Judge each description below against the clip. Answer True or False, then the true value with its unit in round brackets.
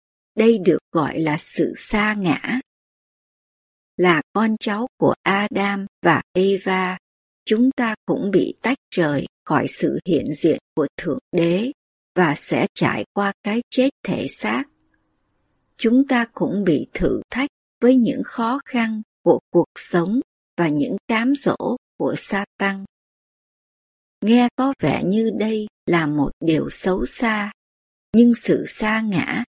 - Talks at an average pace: False (140 wpm)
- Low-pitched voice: False (215 Hz)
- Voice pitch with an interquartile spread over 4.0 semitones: True (4.4 semitones)